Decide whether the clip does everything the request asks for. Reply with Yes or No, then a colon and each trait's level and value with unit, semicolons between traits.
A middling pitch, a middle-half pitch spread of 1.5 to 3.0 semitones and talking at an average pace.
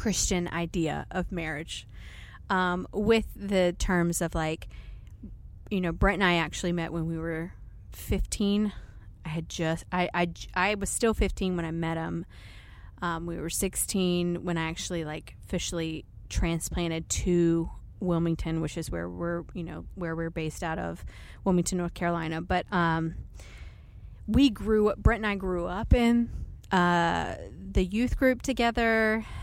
Yes: medium, 170 Hz; average, 2.7 semitones; average, 155 wpm